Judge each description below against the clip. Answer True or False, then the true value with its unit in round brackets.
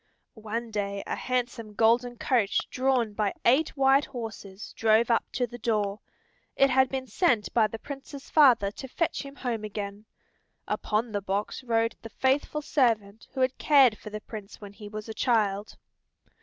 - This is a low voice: False (230 Hz)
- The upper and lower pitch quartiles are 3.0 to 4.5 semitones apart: True (3.5 semitones)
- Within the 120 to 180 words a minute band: True (170 wpm)